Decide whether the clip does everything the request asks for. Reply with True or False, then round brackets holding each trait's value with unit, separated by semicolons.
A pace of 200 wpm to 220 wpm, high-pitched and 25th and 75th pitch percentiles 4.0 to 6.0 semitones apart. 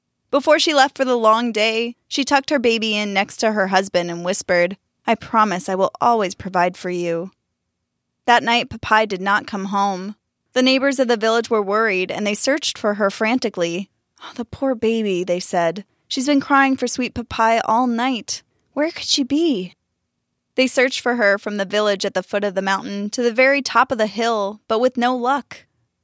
True (205 wpm; 220 Hz; 4.4 semitones)